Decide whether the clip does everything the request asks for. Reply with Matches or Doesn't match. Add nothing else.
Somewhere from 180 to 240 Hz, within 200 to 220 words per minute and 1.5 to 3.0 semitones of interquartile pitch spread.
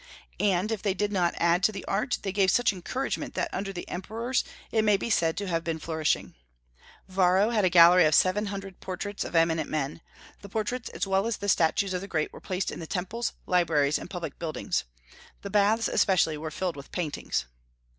Doesn't match